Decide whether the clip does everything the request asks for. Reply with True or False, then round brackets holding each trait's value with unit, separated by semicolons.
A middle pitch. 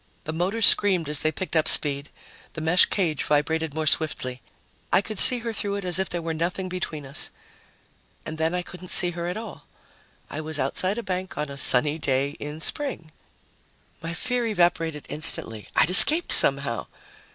True (165 Hz)